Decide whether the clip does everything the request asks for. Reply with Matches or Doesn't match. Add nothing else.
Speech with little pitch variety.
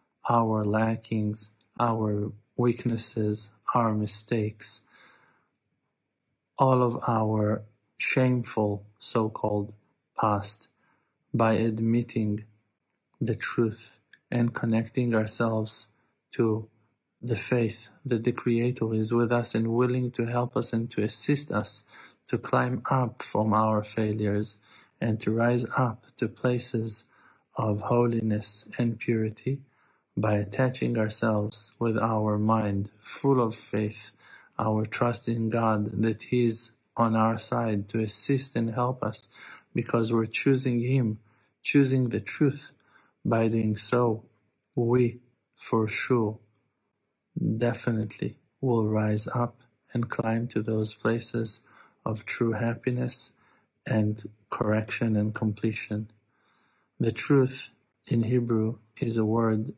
Matches